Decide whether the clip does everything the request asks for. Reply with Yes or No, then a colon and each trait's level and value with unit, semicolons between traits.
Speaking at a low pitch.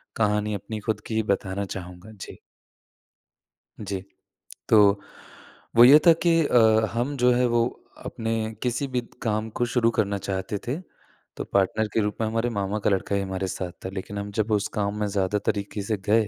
Yes: low, 105 Hz